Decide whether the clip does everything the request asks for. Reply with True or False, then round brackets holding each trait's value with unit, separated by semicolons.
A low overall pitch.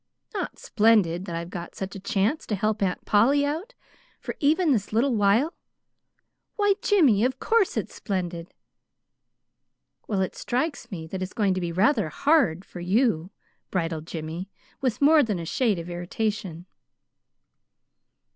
False (205 Hz)